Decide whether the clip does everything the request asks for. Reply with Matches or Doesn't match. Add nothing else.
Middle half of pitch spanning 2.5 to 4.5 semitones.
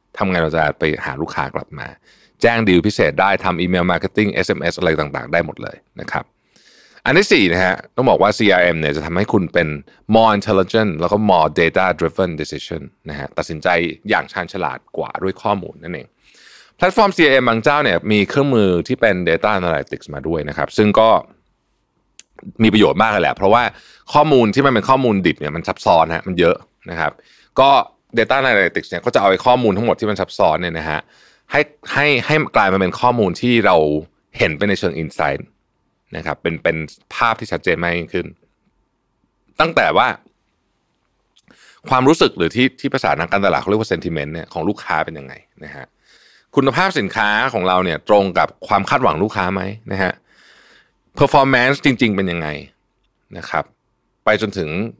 Doesn't match